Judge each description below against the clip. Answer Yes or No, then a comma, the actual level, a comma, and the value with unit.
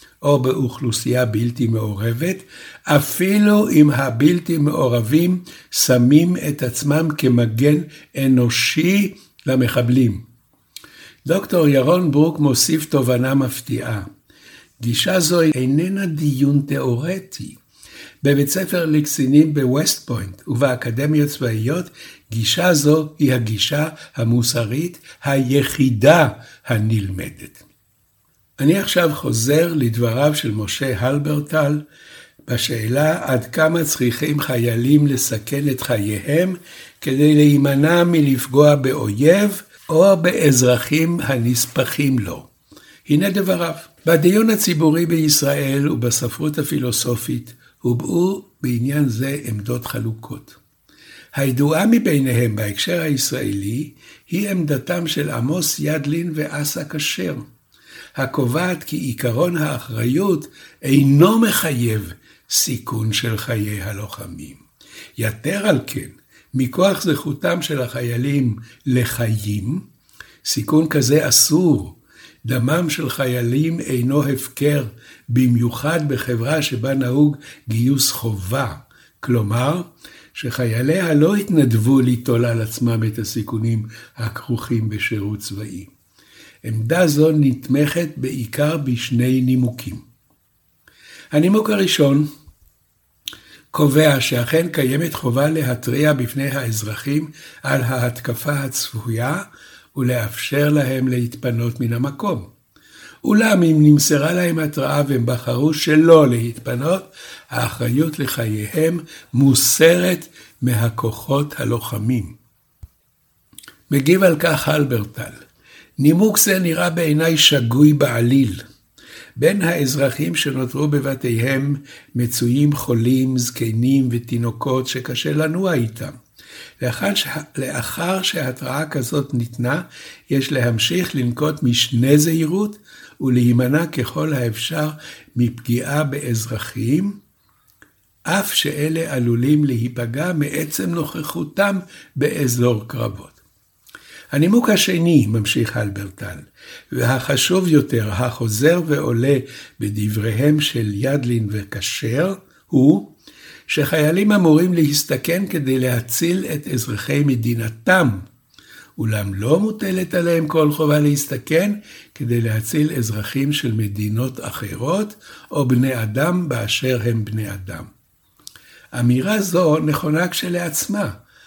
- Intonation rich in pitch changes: No, average, 4.4 semitones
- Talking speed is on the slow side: Yes, slow, 90 wpm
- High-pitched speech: No, medium, 140 Hz